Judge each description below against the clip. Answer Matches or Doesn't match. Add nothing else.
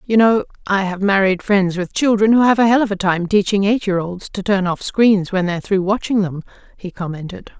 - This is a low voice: Doesn't match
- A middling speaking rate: Doesn't match